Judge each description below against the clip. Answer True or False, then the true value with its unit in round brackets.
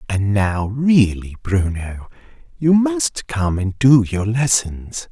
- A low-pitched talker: True (115 Hz)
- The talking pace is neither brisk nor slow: False (130 wpm)